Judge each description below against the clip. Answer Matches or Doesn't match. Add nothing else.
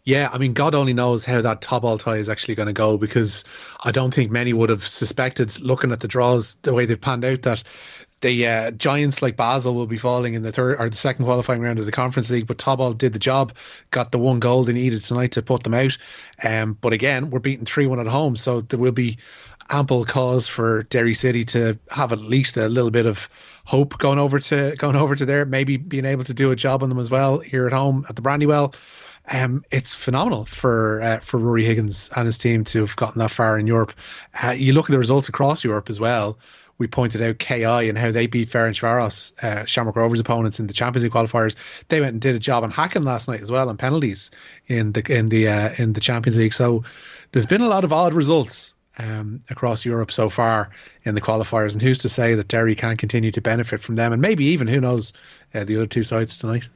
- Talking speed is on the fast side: Matches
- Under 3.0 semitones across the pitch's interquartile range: Matches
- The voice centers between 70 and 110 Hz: Doesn't match